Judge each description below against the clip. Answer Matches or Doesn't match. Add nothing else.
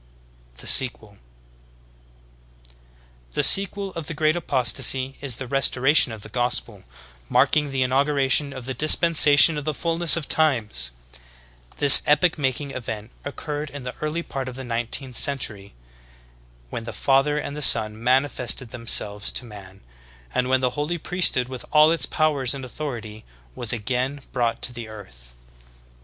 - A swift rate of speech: Doesn't match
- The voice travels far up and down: Doesn't match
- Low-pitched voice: Matches